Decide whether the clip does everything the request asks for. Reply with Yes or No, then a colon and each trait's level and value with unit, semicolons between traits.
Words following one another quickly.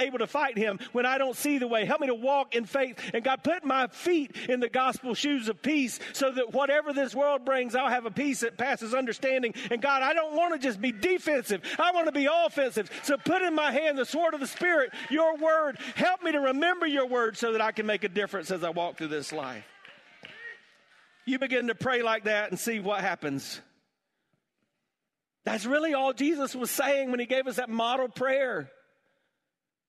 Yes: fast, 215 wpm